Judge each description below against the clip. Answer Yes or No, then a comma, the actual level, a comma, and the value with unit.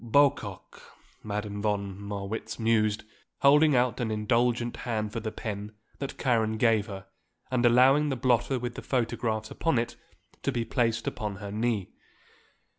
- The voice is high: No, low, 115 Hz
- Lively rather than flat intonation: No, narrow, 2.5 semitones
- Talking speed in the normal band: Yes, average, 150 wpm